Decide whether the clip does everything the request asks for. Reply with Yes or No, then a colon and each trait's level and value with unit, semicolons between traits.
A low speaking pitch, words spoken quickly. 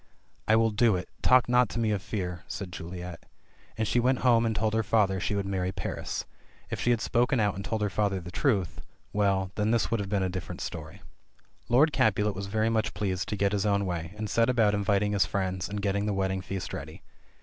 Yes: low, 105 Hz; fast, 235 wpm